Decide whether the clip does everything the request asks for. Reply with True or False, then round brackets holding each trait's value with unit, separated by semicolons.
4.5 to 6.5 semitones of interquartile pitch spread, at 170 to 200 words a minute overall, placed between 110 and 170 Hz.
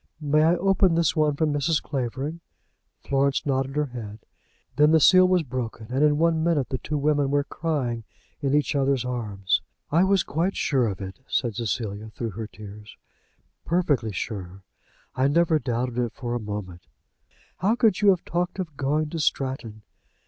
True (5.4 semitones; 175 wpm; 140 Hz)